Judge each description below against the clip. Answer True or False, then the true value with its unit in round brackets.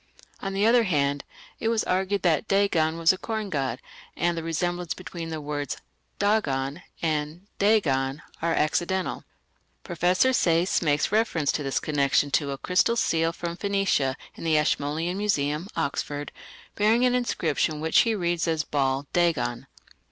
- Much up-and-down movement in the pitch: False (4.8 semitones)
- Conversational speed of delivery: True (155 wpm)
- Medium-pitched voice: True (165 Hz)